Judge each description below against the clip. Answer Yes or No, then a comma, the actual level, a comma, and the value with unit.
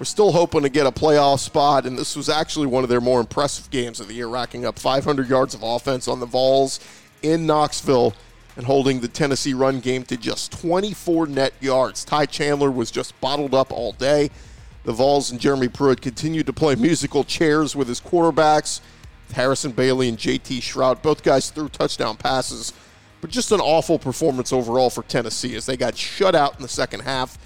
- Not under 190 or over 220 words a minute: Yes, average, 200 wpm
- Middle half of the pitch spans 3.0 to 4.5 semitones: Yes, average, 3.5 semitones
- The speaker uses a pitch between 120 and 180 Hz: Yes, low, 135 Hz